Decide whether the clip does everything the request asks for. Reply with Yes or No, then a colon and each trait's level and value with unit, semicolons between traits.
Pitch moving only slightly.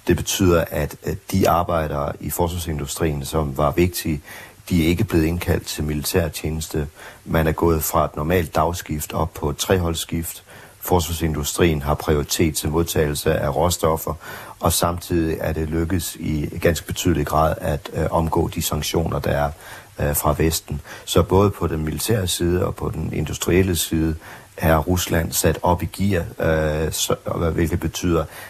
Yes: narrow, 2.2 semitones